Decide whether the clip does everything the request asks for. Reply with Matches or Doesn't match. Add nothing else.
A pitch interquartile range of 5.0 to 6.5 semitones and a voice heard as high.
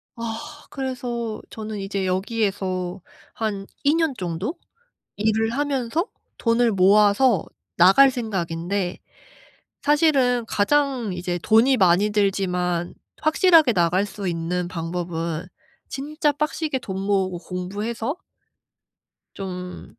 Matches